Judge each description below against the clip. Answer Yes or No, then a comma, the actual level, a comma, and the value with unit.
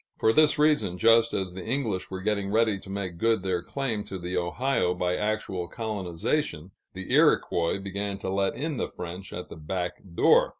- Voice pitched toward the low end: Yes, very low, 95 Hz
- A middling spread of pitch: Yes, average, 3.9 semitones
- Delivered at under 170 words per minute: No, average, 185 wpm